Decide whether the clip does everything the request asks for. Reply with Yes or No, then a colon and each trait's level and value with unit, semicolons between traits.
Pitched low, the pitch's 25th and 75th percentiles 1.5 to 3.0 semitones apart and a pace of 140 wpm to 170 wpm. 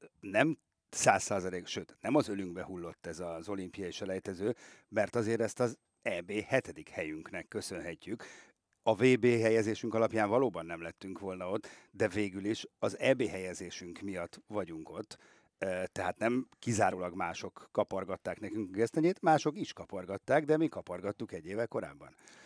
No: low, 100 Hz; average, 4.0 semitones; average, 145 wpm